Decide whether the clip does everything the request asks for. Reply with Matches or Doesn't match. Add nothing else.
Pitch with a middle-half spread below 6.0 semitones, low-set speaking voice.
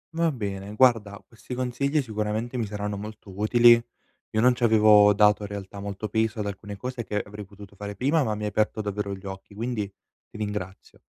Matches